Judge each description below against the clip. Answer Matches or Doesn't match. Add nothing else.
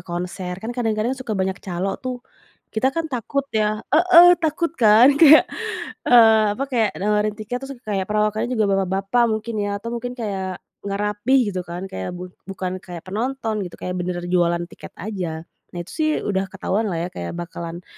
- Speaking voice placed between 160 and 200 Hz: Doesn't match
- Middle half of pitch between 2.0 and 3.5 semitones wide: Doesn't match